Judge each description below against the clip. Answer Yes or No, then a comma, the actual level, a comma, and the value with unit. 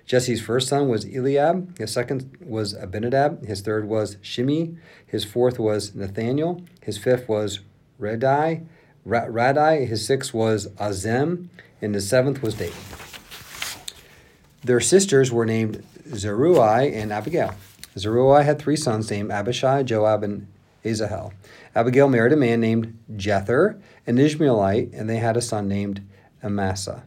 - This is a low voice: Yes, low, 115 Hz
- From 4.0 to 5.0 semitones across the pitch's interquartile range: Yes, average, 4.5 semitones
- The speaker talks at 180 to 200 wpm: No, slow, 135 wpm